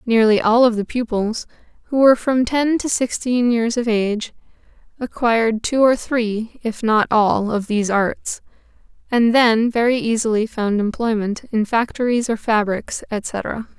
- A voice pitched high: Yes, high, 230 Hz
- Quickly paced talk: No, average, 150 wpm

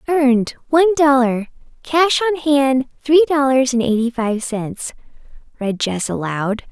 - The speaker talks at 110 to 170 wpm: Yes, slow, 135 wpm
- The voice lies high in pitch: Yes, very high, 265 Hz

